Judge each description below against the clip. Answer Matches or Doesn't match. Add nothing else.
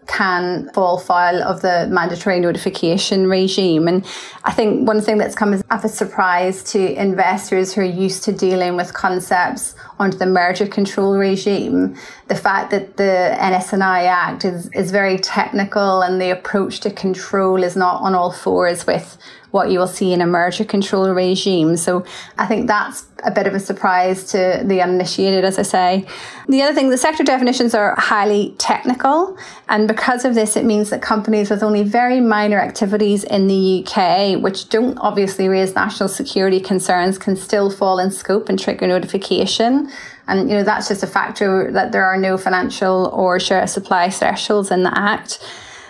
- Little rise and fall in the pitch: Matches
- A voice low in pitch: Doesn't match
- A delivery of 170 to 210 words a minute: Matches